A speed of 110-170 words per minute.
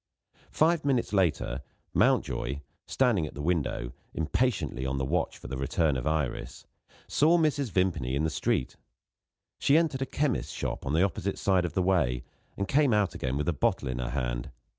No: average, 185 wpm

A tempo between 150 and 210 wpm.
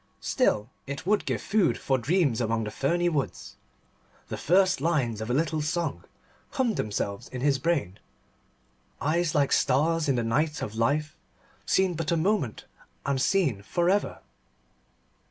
Yes: average, 155 wpm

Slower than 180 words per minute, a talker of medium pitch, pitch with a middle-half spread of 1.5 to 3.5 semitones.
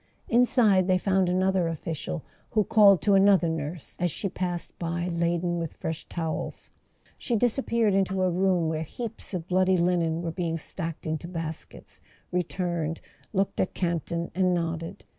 Yes: average, 155 wpm; medium, 175 Hz; narrow, 2.4 semitones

